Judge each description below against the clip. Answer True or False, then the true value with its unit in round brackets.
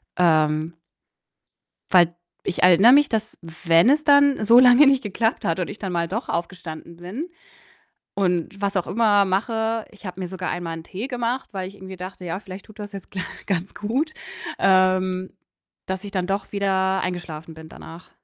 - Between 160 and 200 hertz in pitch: True (190 Hz)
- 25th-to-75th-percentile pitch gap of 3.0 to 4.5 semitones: True (3.5 semitones)